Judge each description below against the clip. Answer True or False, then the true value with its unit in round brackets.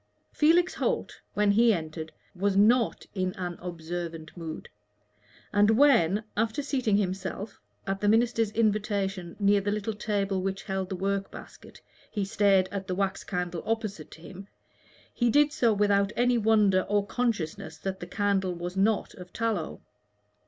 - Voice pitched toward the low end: False (200 Hz)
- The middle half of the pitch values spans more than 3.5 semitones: False (2.9 semitones)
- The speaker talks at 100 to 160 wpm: True (155 wpm)